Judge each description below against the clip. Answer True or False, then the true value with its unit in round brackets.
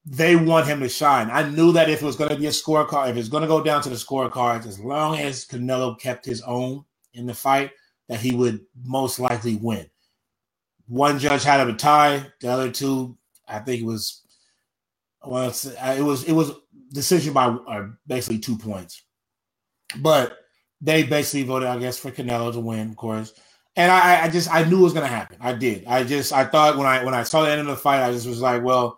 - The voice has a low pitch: True (130 Hz)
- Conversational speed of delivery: False (225 wpm)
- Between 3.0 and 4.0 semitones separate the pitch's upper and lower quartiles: True (3.5 semitones)